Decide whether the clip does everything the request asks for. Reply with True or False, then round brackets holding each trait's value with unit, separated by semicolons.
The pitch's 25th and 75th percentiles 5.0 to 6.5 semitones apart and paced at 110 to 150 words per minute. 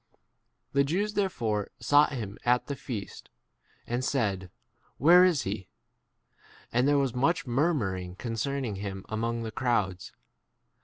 True (5.3 semitones; 140 wpm)